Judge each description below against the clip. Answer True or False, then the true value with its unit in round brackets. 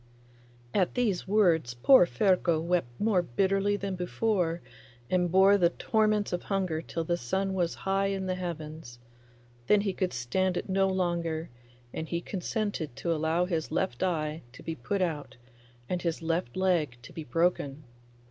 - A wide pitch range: False (3.1 semitones)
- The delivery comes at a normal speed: True (165 wpm)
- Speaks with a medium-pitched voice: True (175 Hz)